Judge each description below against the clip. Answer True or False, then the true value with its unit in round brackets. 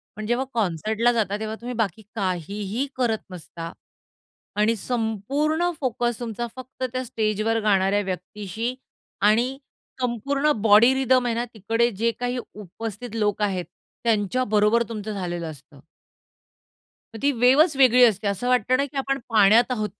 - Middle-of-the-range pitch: False (225 Hz)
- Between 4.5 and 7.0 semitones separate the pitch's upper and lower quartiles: False (3.3 semitones)